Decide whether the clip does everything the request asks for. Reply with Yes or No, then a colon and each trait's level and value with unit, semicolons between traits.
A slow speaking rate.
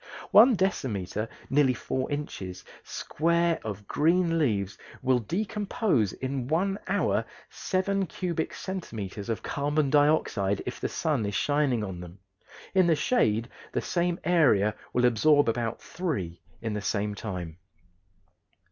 Yes: slow, 130 wpm